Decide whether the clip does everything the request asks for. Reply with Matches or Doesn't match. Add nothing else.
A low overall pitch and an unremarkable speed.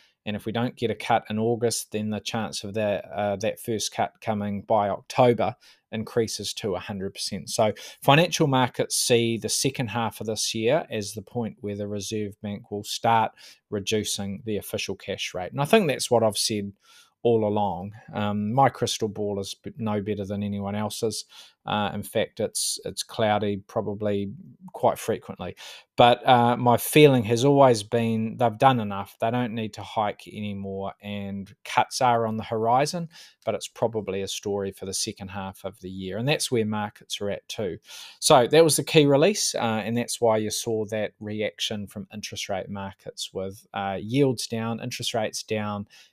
Matches